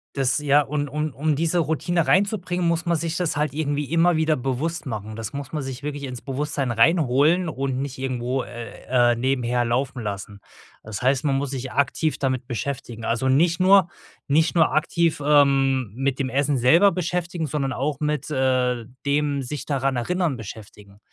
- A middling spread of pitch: Yes, average, 3.7 semitones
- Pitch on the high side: No, medium, 140 Hz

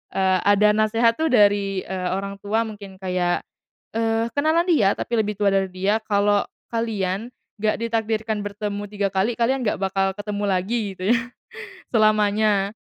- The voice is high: Yes, high, 205 Hz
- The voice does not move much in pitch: Yes, narrow, 2.3 semitones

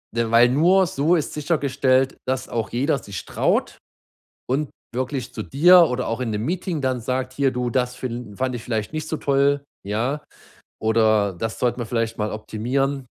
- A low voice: Yes, low, 130 Hz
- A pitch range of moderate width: Yes, average, 3.5 semitones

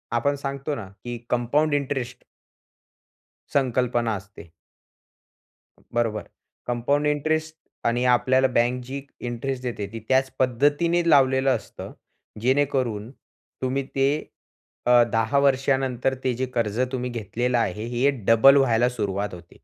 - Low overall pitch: Yes, low, 125 Hz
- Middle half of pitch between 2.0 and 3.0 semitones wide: Yes, average, 2.7 semitones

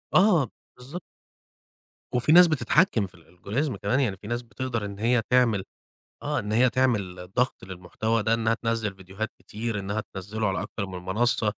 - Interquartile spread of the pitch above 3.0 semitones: Yes, average, 4.2 semitones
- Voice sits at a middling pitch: No, low, 110 Hz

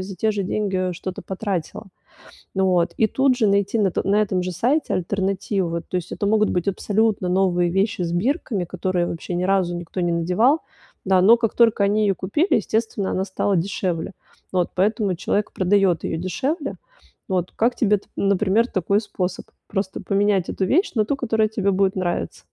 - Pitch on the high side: Yes, high, 195 Hz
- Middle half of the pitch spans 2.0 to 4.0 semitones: Yes, average, 2.8 semitones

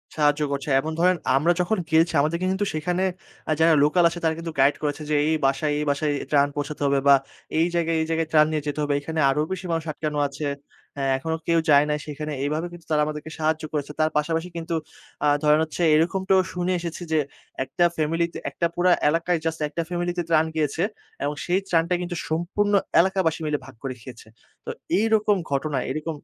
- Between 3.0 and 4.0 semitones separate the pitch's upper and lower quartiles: No, narrow, 2.5 semitones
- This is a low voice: No, medium, 160 Hz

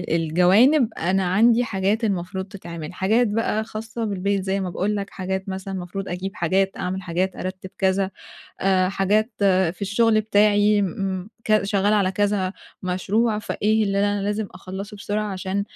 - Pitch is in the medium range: No, high, 195 Hz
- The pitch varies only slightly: Yes, narrow, 2.0 semitones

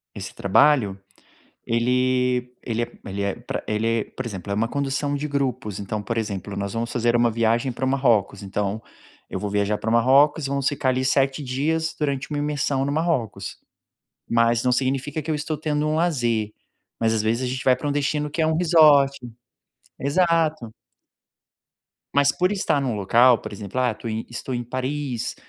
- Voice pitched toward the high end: No, low, 130 Hz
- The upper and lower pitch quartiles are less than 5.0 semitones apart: Yes, average, 4.2 semitones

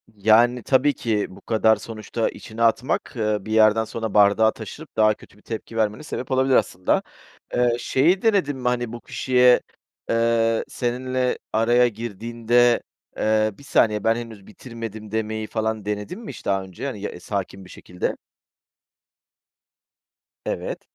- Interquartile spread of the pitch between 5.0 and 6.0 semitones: No, narrow, 2.4 semitones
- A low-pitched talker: Yes, low, 115 Hz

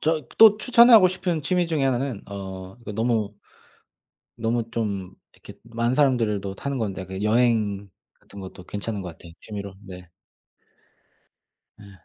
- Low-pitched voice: Yes, low, 110 Hz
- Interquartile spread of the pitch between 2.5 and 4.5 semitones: No, wide, 5.6 semitones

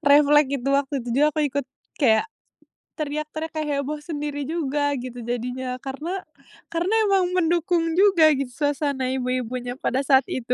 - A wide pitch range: No, average, 3.2 semitones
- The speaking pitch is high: Yes, very high, 285 Hz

